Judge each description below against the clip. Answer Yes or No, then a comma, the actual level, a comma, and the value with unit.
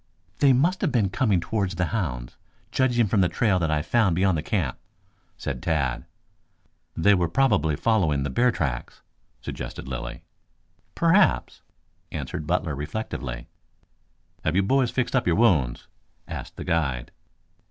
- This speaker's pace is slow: No, average, 145 wpm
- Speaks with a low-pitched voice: Yes, very low, 90 Hz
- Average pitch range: No, wide, 7.5 semitones